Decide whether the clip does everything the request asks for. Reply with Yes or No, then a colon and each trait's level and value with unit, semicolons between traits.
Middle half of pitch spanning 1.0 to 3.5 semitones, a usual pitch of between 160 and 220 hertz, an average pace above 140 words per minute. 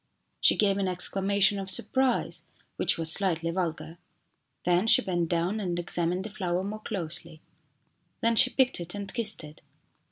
Yes: average, 3.0 semitones; medium, 185 Hz; average, 160 wpm